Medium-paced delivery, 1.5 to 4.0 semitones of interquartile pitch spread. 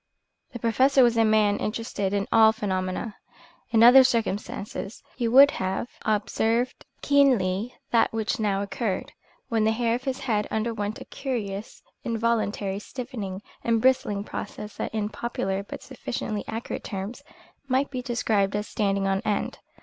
Yes: average, 150 wpm; average, 2.8 semitones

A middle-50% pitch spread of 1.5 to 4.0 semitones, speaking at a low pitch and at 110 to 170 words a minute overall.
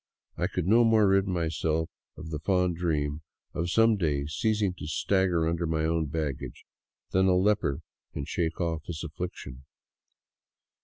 Yes: average, 3.3 semitones; very low, 85 Hz; average, 155 wpm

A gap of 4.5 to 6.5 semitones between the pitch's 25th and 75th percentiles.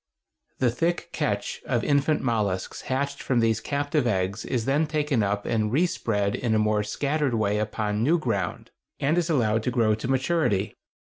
Yes: average, 5.0 semitones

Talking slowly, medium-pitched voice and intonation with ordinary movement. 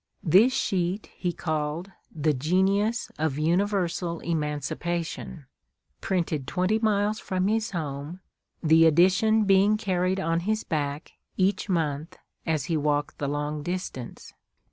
Yes: slow, 120 wpm; medium, 175 Hz; average, 4.2 semitones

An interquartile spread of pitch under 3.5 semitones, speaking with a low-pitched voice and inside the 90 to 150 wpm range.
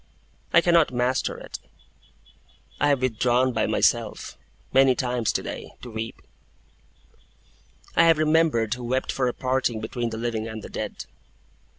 Yes: narrow, 2.6 semitones; low, 125 Hz; average, 145 wpm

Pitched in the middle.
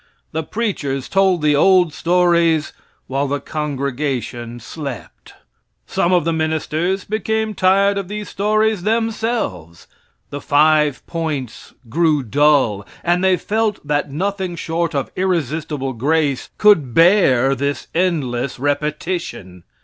Yes: medium, 160 Hz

